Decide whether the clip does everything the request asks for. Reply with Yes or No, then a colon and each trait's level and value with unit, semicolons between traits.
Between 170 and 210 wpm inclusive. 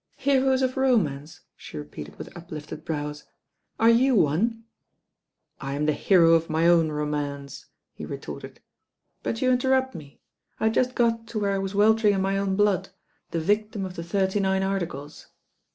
Yes: average, 180 wpm